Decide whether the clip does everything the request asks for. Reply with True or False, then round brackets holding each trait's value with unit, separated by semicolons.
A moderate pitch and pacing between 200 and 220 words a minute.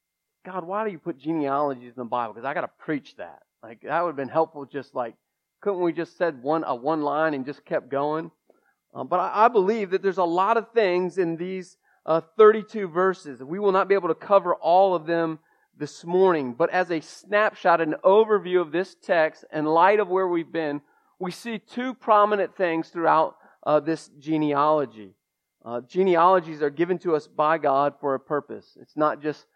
True (170 Hz; 205 wpm)